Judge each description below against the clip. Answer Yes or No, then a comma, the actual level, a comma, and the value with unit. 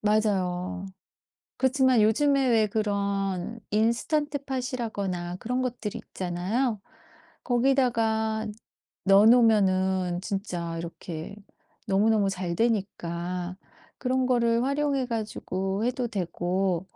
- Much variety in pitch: No, average, 4.5 semitones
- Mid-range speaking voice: No, high, 215 Hz